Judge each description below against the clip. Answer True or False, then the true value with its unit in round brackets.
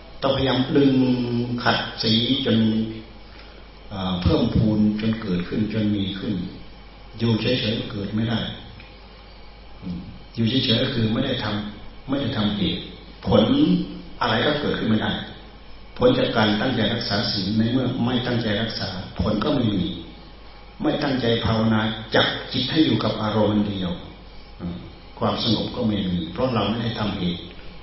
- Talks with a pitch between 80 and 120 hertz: True (110 Hz)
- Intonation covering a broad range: False (2.4 semitones)